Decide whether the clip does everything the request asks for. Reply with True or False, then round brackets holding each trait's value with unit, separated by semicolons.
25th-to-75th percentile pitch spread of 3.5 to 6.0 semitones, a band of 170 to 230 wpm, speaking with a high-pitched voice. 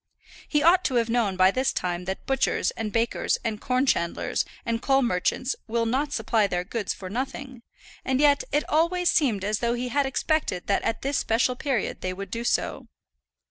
True (4.7 semitones; 195 wpm; 235 Hz)